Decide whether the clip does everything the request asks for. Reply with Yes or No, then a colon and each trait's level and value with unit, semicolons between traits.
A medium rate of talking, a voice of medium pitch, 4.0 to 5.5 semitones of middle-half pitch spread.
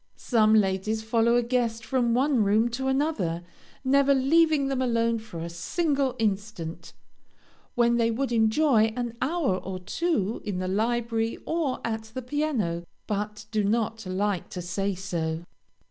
No: average, 150 wpm; high, 230 Hz; average, 4.3 semitones